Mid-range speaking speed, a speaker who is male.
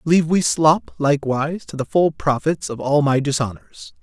Yes: average, 180 wpm; male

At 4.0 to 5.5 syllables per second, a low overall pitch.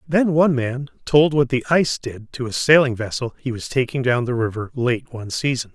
Yes: 5.4 syllables/s; low, 130 Hz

